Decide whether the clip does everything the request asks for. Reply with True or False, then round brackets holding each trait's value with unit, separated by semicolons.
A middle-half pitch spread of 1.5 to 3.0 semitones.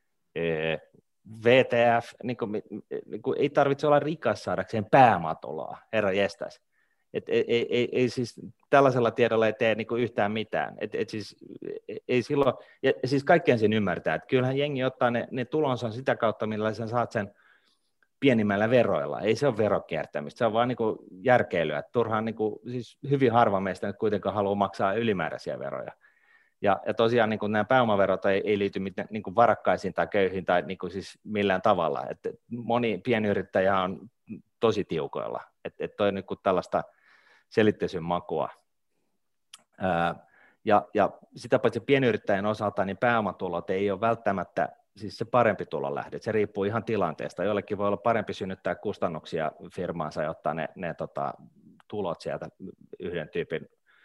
False (3.8 semitones)